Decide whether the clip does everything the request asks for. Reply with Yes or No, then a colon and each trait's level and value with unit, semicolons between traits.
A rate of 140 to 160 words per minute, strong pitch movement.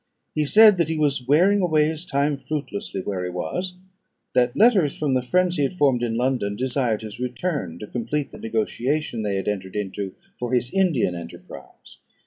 No: average, 185 wpm; wide, 6.0 semitones